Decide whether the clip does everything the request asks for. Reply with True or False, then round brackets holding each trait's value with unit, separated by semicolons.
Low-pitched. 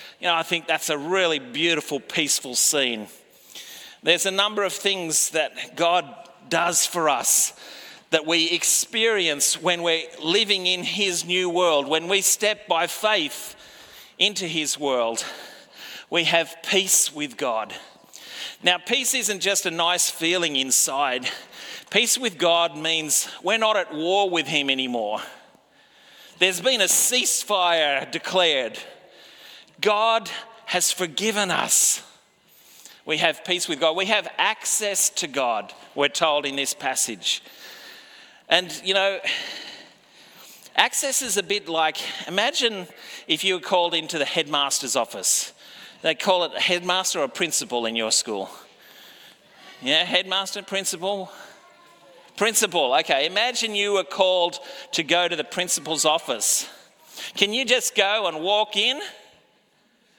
False (180 Hz)